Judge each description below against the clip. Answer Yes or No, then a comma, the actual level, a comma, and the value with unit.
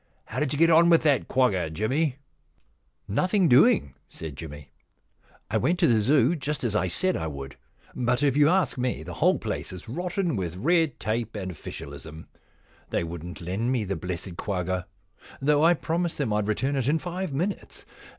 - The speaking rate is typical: Yes, average, 195 wpm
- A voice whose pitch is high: No, low, 125 Hz